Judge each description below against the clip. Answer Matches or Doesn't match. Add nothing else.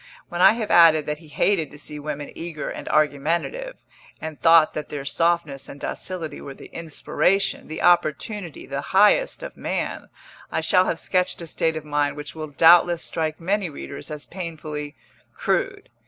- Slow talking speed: Doesn't match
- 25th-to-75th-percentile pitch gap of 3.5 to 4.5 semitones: Doesn't match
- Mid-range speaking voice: Matches